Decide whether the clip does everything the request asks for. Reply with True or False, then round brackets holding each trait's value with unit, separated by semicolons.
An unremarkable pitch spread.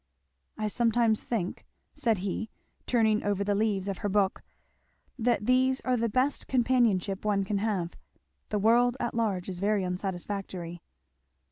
True (3.2 semitones)